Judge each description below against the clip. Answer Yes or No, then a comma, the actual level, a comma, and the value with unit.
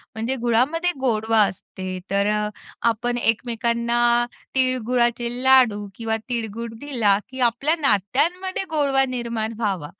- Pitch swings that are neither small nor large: Yes, average, 3.0 semitones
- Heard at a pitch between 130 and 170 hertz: No, high, 235 Hz